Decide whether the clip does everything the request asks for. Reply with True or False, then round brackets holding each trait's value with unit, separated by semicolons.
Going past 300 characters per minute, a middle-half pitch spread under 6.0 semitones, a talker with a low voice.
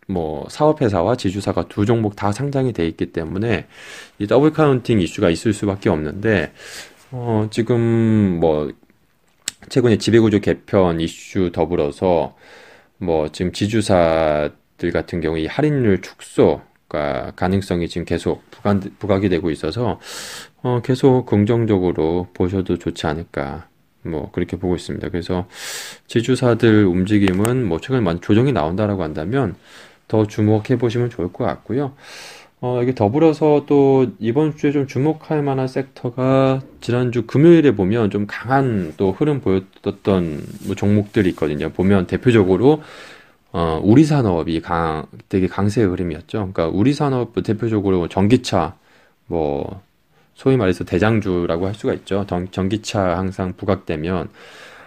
False (295 characters per minute; 5.5 semitones; 100 Hz)